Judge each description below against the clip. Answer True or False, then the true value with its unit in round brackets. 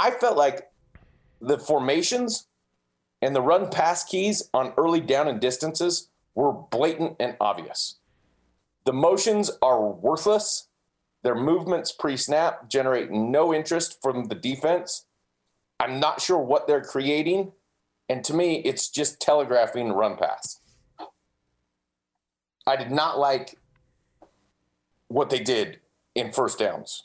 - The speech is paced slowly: True (125 wpm)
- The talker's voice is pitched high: False (135 Hz)